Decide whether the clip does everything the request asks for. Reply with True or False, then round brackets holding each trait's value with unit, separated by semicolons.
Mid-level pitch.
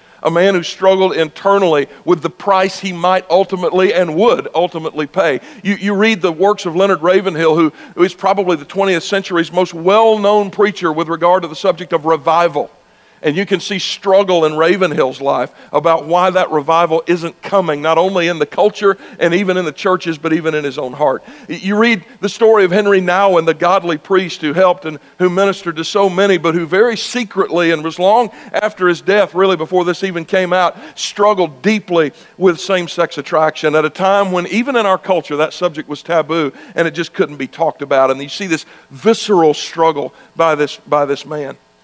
True (180 Hz)